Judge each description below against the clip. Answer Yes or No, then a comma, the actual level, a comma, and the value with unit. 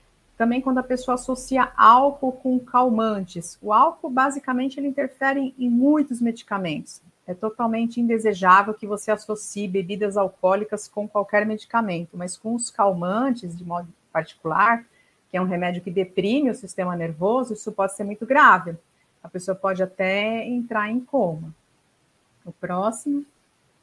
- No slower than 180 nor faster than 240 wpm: No, average, 145 wpm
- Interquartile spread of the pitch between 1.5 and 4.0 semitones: No, average, 5.0 semitones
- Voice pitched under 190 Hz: No, high, 210 Hz